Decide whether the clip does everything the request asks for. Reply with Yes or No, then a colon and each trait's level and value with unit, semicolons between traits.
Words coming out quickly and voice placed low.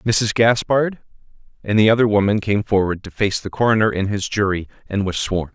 No: average, 195 wpm; low, 105 Hz